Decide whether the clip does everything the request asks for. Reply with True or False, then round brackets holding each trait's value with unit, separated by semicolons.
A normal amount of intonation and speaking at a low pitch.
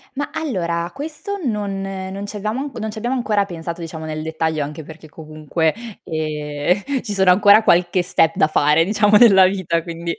False (4.7 semitones; 185 Hz)